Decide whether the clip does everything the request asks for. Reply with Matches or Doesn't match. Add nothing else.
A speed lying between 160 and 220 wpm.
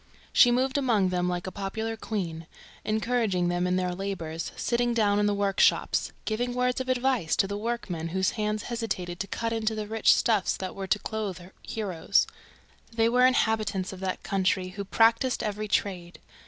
Matches